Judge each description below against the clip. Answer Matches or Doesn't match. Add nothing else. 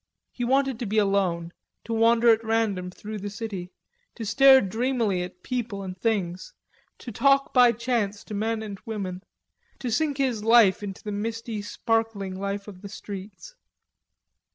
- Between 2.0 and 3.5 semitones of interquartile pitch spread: Matches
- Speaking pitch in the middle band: Doesn't match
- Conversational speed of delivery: Matches